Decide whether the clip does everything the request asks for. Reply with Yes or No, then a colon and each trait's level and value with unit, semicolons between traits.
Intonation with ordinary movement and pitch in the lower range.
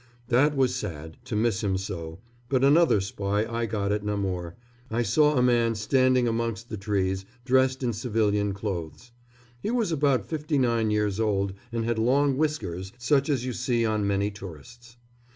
Yes: average, 4.3 semitones; low, 115 Hz